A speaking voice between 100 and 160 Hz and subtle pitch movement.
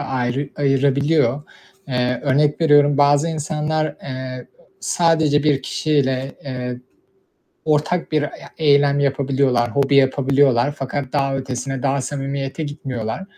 Yes: medium, 140 Hz; narrow, 1.9 semitones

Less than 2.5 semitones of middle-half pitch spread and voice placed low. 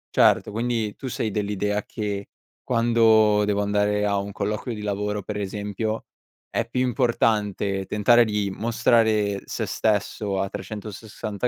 Yes: narrow, 1.6 semitones; low, 105 Hz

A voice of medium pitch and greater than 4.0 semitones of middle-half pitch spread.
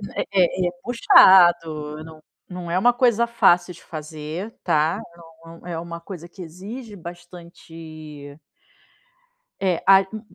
No: medium, 175 Hz; average, 3.1 semitones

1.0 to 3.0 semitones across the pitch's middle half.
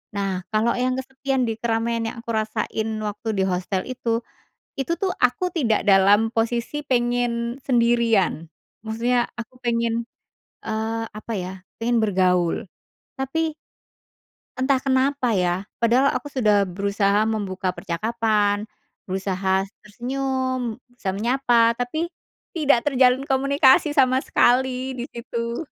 No: average, 3.6 semitones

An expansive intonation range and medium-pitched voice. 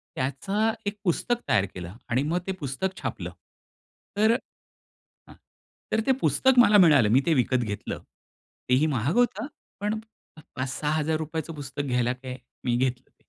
Yes: wide, 7.8 semitones; medium, 150 Hz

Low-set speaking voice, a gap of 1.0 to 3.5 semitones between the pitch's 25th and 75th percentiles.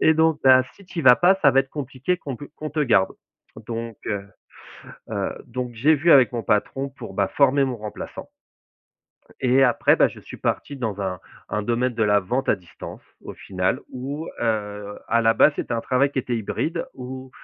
No: low, 125 Hz; average, 3.9 semitones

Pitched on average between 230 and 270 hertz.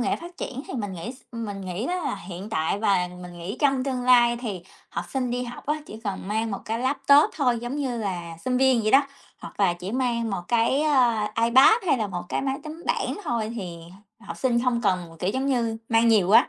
Yes: high, 235 Hz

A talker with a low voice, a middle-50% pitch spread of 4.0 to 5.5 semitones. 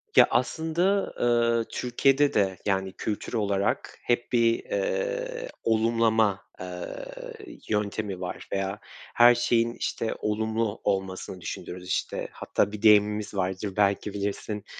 No: low, 110 Hz; average, 3.4 semitones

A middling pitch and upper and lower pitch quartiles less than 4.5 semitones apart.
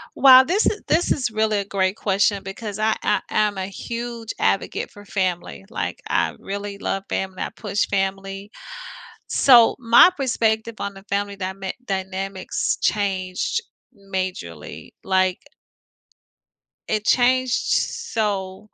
No: high, 200 Hz; average, 2.7 semitones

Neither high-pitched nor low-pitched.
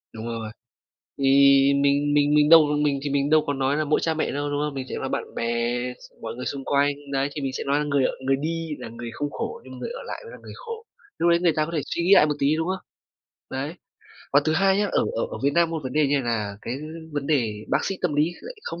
Yes: medium, 145 Hz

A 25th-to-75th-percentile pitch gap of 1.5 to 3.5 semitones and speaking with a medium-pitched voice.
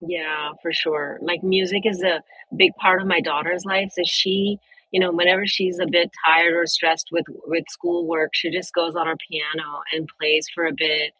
Yes: narrow, 2.6 semitones; medium, 170 Hz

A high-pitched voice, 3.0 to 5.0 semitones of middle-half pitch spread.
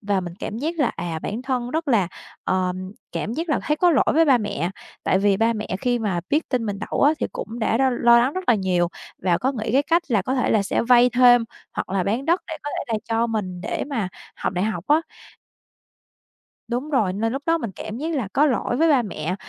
No: high, 235 Hz; wide, 5.6 semitones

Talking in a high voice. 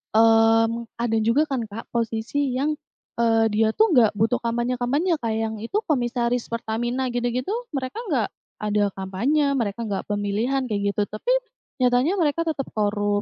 Yes: high, 235 Hz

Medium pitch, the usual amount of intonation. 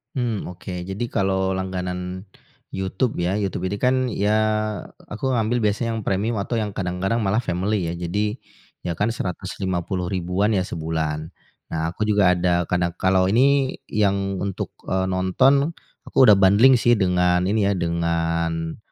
No: very low, 95 Hz; average, 3.1 semitones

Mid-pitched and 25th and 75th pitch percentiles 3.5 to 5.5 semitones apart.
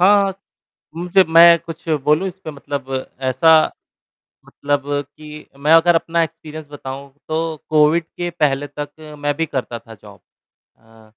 No: medium, 155 Hz; average, 2.8 semitones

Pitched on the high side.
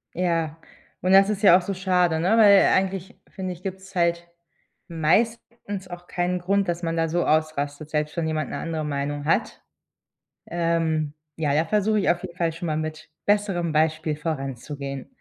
No: medium, 170 Hz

